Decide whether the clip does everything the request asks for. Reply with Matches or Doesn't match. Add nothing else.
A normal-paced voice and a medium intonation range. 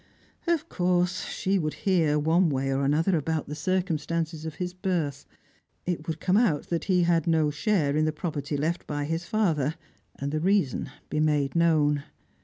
Matches